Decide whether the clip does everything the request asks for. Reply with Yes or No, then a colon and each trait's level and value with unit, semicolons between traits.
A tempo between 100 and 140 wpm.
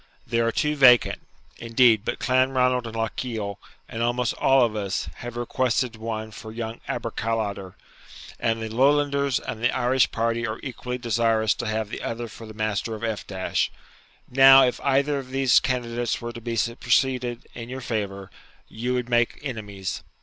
No: average, 165 wpm